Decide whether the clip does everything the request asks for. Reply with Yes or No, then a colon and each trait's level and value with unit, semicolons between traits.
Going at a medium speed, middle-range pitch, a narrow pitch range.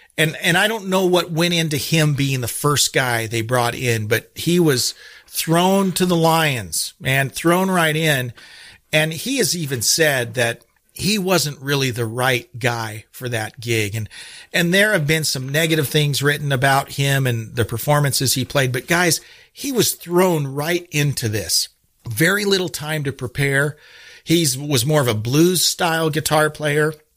No: average, 175 wpm; medium, 150 Hz; average, 4.6 semitones